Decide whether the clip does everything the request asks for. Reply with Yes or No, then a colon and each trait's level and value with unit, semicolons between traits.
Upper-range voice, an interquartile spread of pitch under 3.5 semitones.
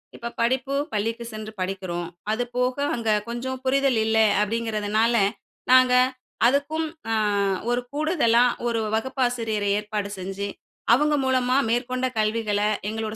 Yes: high, 235 Hz; average, 3.1 semitones